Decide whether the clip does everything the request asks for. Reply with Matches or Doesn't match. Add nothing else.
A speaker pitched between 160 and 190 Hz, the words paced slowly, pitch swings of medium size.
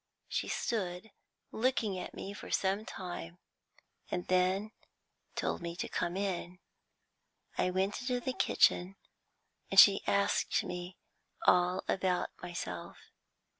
Doesn't match